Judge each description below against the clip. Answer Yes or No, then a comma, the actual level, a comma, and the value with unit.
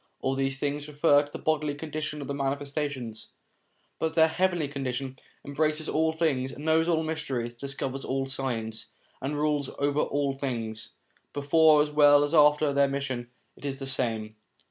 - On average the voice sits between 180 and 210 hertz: No, medium, 145 Hz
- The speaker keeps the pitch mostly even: Yes, narrow, 2.2 semitones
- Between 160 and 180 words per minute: Yes, average, 165 wpm